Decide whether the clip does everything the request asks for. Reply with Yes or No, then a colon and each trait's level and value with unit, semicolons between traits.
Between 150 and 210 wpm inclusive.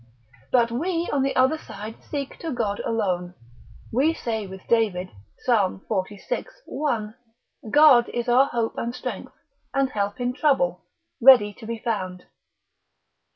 No: average, 140 wpm